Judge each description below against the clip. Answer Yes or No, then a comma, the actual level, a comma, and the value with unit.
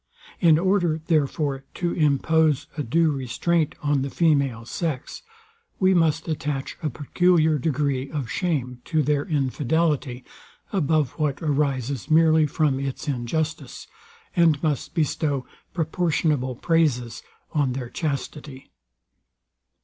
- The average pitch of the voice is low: No, medium, 150 Hz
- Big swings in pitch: No, average, 3.0 semitones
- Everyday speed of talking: No, slow, 115 wpm